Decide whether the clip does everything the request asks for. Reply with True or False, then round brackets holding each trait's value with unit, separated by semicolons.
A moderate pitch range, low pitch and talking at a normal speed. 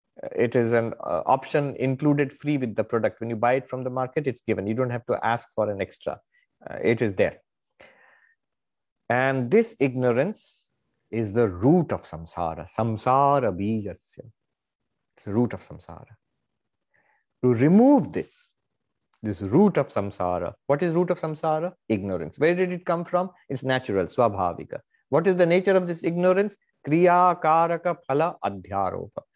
False (7.5 semitones; 130 Hz; 160 wpm)